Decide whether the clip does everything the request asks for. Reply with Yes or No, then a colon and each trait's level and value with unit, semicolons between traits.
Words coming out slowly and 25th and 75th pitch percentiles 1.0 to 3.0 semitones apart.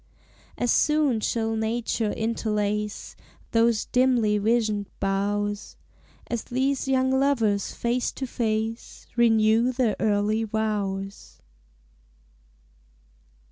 Yes: slow, 90 wpm; narrow, 2.5 semitones